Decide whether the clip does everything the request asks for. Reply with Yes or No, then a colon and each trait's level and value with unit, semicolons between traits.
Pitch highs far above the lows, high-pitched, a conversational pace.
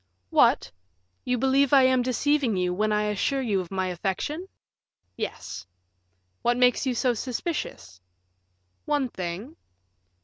No: wide, 5.8 semitones; high, 245 Hz; slow, 130 wpm